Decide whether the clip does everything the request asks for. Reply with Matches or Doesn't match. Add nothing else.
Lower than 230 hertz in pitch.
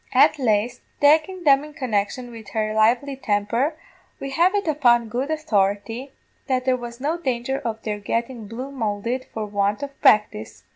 Doesn't match